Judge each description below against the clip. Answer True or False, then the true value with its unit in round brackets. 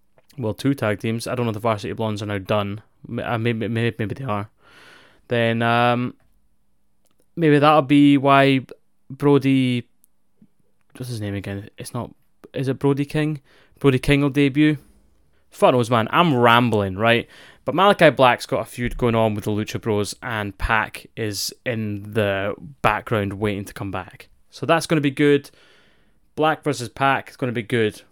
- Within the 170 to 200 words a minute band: True (175 wpm)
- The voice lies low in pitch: True (120 Hz)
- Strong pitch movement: False (4.7 semitones)